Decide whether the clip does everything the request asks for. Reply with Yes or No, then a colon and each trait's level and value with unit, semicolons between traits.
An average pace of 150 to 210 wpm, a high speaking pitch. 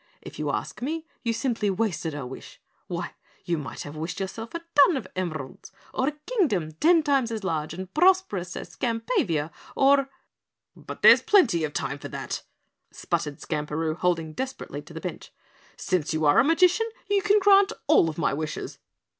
Yes: average, 180 wpm; high, 200 Hz